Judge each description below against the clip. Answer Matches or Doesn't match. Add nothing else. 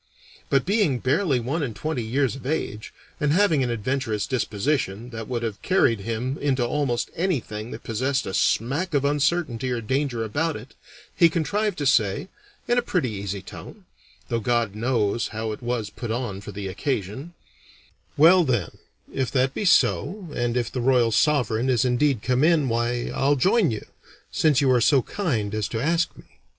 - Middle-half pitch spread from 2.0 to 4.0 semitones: Doesn't match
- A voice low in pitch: Matches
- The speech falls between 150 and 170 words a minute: Doesn't match